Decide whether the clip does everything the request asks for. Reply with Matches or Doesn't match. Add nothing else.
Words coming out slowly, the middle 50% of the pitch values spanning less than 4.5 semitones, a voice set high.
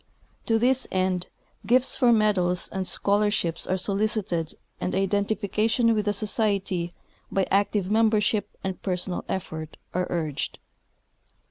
Matches